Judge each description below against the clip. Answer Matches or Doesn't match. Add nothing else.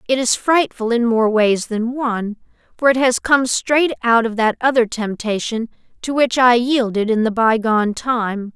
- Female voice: Matches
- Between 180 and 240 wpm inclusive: Matches